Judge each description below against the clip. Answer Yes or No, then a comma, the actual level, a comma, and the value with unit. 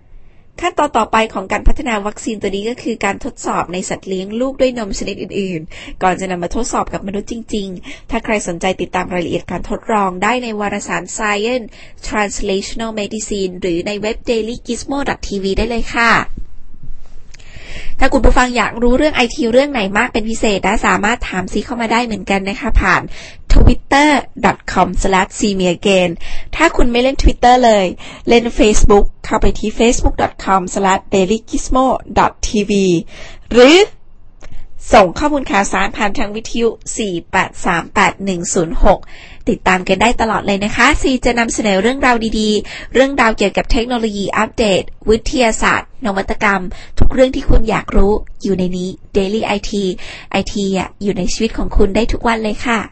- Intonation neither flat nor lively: Yes, average, 3.5 semitones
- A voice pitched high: Yes, high, 215 Hz